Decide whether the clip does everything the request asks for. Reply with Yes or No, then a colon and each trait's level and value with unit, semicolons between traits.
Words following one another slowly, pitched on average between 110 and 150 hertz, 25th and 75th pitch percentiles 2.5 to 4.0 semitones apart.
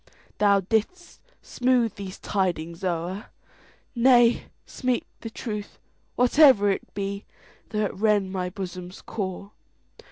No: slow, 100 wpm; high, 205 Hz; average, 3.7 semitones